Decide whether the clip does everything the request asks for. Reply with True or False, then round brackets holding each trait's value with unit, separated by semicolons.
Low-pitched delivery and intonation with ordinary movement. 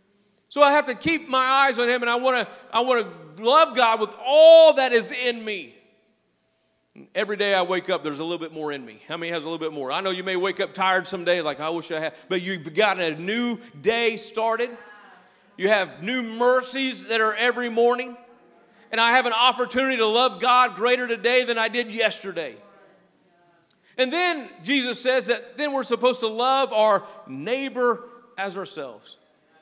False (230 Hz; 4.8 semitones)